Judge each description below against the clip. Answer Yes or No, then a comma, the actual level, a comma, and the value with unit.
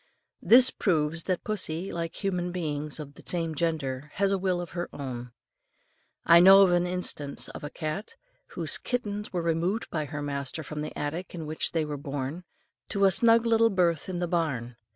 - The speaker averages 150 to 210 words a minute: Yes, average, 190 wpm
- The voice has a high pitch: No, medium, 170 Hz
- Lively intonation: No, average, 3.8 semitones